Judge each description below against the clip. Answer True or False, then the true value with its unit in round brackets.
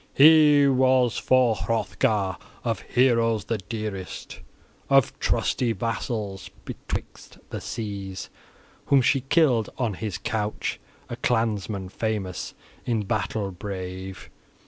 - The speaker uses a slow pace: True (105 wpm)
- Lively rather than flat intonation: False (4.1 semitones)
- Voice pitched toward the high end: False (110 Hz)